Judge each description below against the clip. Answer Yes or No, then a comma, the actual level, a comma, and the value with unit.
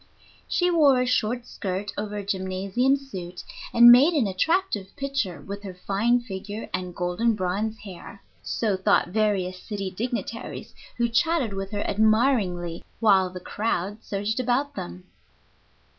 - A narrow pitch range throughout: No, average, 4.3 semitones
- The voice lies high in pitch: Yes, high, 210 Hz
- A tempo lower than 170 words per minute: Yes, average, 145 wpm